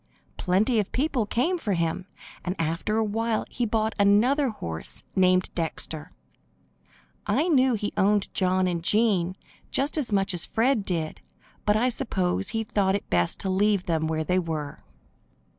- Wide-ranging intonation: No, average, 4.0 semitones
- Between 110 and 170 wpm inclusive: Yes, average, 160 wpm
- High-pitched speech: Yes, high, 200 Hz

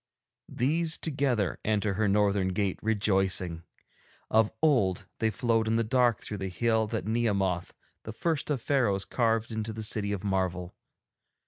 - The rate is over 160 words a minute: No, average, 150 wpm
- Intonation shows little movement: No, average, 3.1 semitones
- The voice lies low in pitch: Yes, low, 110 Hz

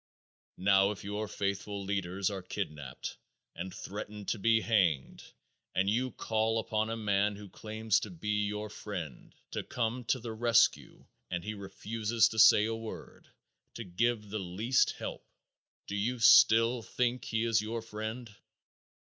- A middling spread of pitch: No, narrow, 2.2 semitones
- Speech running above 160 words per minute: No, average, 155 wpm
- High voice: No, low, 105 Hz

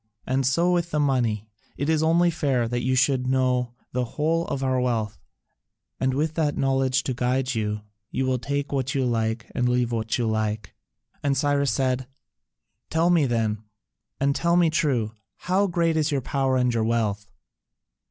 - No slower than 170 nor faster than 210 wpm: Yes, average, 180 wpm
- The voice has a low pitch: Yes, low, 130 Hz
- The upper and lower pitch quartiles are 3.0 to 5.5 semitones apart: Yes, average, 3.4 semitones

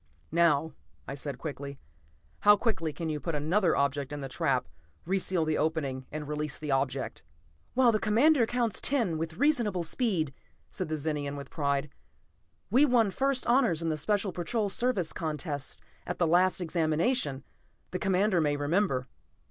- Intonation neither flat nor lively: No, wide, 5.9 semitones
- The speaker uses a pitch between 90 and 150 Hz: No, medium, 165 Hz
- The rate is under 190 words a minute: Yes, average, 160 wpm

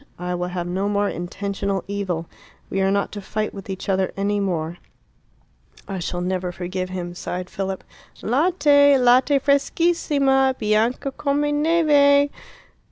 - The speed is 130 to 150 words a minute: Yes, average, 140 wpm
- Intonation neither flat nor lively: No, wide, 7.3 semitones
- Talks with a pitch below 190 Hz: No, high, 200 Hz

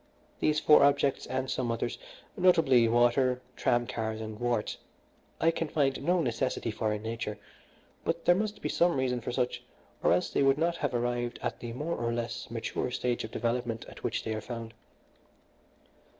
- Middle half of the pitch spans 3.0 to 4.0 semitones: Yes, average, 3.6 semitones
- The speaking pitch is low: Yes, low, 120 Hz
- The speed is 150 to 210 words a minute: Yes, average, 180 wpm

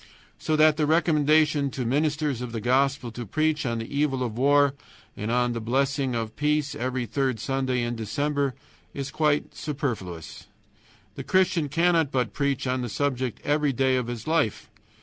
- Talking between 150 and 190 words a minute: Yes, average, 170 wpm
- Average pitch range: Yes, average, 3.5 semitones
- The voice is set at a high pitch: No, low, 135 Hz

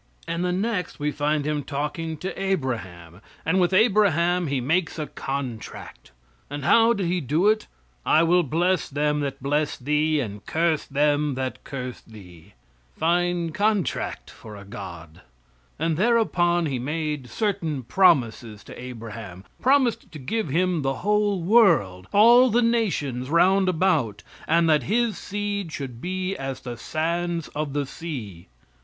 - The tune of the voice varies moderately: No, wide, 5.8 semitones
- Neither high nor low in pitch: Yes, medium, 155 Hz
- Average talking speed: Yes, average, 150 wpm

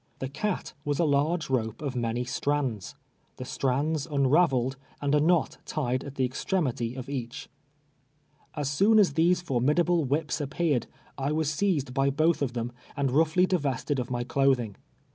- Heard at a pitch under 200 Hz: Yes, medium, 140 Hz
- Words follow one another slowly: No, average, 175 wpm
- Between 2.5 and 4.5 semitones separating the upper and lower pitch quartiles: Yes, average, 3.7 semitones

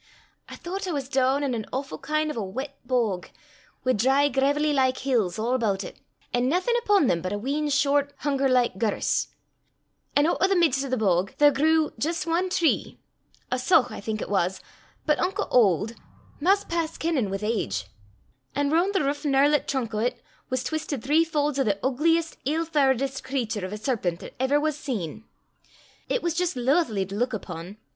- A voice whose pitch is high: Yes, very high, 270 Hz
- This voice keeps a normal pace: Yes, average, 195 wpm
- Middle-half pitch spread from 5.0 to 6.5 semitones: Yes, average, 5.3 semitones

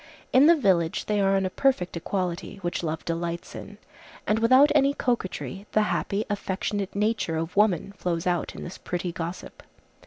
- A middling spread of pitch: Yes, average, 3.6 semitones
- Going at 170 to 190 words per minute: Yes, average, 175 wpm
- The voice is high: Yes, high, 195 Hz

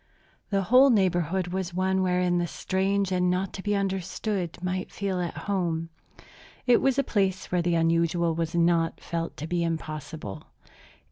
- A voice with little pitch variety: Yes, narrow, 2.3 semitones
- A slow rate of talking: No, average, 165 wpm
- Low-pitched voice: No, medium, 180 Hz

